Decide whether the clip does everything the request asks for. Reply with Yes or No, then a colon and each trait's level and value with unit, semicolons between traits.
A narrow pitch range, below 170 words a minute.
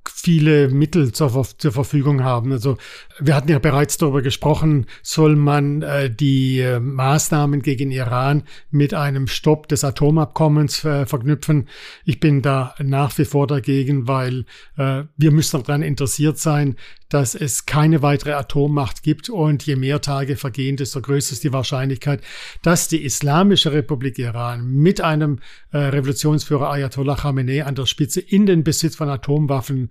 Yes: narrow, 1.9 semitones; average, 155 wpm